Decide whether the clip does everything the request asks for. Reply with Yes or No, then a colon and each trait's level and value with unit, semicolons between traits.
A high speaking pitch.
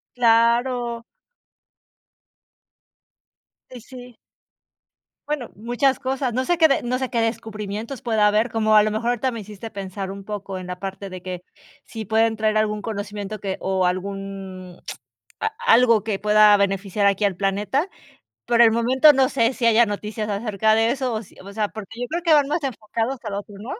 Yes: high, 220 Hz